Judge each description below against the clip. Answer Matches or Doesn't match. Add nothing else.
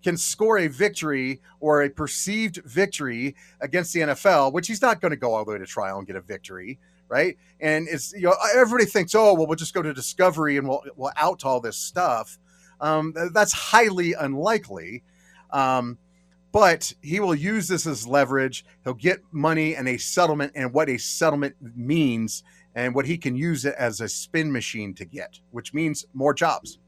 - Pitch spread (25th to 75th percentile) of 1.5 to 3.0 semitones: Doesn't match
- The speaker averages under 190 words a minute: Doesn't match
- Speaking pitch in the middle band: Matches